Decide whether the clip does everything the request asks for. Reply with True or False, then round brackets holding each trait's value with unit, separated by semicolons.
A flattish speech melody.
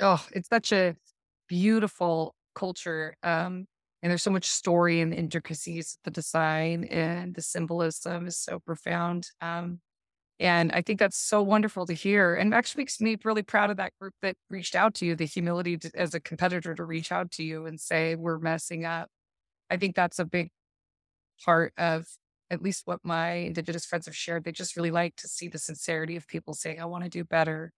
True (1.8 semitones)